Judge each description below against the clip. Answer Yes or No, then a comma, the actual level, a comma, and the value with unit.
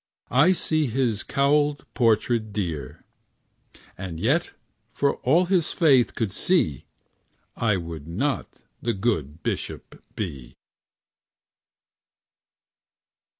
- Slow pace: Yes, slow, 95 wpm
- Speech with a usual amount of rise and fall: No, wide, 8.4 semitones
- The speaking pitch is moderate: No, low, 115 Hz